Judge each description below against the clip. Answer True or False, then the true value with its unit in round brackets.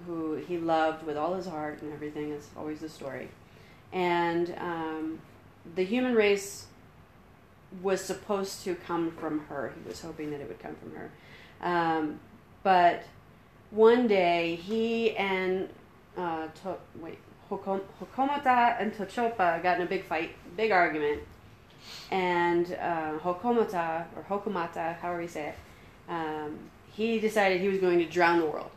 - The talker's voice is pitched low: False (175 Hz)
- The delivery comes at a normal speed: True (150 wpm)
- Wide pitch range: False (3.6 semitones)